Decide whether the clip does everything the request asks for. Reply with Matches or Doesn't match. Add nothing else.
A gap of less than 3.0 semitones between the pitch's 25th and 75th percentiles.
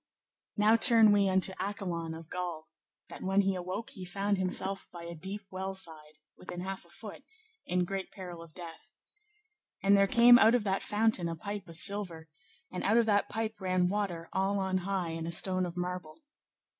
Matches